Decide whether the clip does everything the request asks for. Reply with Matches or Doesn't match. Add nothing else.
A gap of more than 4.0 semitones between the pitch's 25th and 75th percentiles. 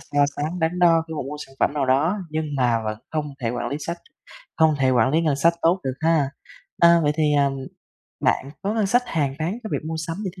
Doesn't match